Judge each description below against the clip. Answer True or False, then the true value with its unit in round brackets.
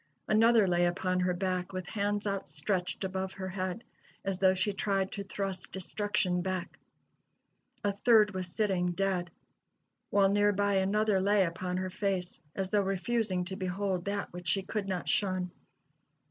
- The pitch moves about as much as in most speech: False (1.8 semitones)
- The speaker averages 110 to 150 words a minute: False (160 wpm)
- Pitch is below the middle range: False (190 Hz)